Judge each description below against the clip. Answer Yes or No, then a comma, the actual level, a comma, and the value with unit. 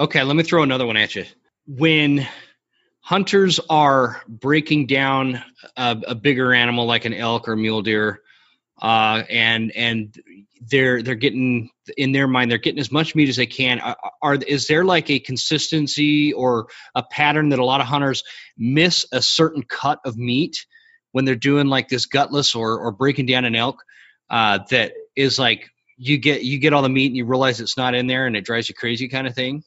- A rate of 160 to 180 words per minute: No, average, 200 wpm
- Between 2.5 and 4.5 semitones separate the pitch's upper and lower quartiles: Yes, average, 3.3 semitones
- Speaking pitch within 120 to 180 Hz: Yes, low, 130 Hz